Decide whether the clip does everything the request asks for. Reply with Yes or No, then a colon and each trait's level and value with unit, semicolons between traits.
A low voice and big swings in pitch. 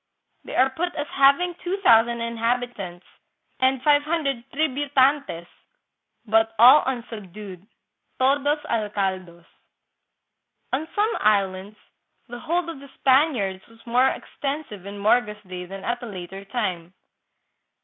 No: high, 240 Hz; wide, 5.8 semitones